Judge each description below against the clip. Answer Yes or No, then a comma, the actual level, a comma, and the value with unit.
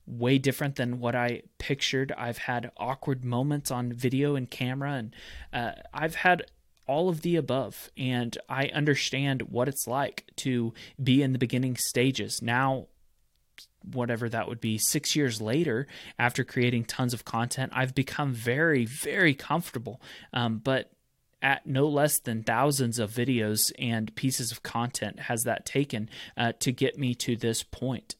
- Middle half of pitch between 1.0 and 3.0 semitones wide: Yes, narrow, 2.5 semitones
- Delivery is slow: No, average, 160 wpm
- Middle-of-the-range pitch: No, low, 125 Hz